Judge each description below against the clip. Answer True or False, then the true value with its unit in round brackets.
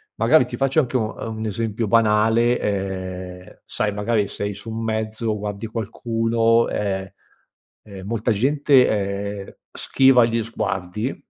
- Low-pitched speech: True (110 Hz)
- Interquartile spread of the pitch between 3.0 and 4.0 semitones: False (2.5 semitones)